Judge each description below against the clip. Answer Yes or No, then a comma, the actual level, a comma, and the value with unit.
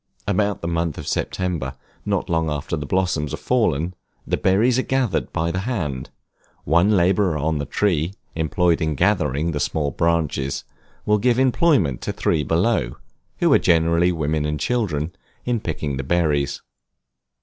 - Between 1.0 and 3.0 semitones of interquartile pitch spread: No, average, 4.6 semitones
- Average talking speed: Yes, average, 160 wpm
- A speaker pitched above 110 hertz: No, very low, 85 Hz